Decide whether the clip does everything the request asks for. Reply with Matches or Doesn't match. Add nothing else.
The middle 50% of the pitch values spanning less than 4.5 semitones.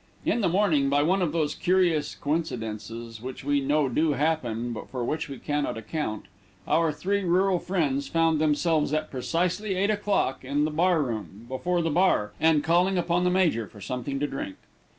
Doesn't match